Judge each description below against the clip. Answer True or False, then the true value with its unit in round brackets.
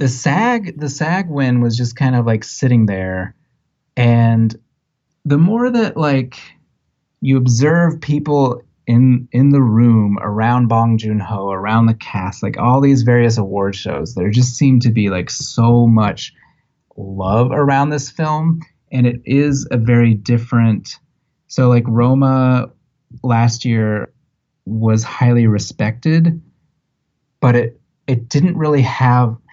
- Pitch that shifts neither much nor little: True (4.1 semitones)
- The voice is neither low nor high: False (125 Hz)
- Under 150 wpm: True (140 wpm)